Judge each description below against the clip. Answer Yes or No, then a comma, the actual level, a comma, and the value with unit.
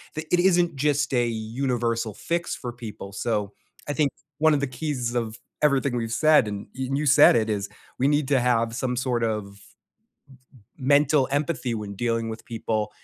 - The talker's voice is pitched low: Yes, low, 125 Hz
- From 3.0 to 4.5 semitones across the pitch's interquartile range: Yes, average, 4.1 semitones